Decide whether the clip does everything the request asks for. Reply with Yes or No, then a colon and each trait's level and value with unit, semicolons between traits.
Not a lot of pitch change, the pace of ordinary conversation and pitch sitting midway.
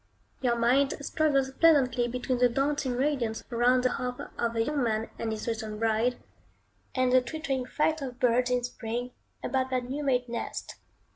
No: narrow, 2.3 semitones; average, 170 wpm; very high, 250 Hz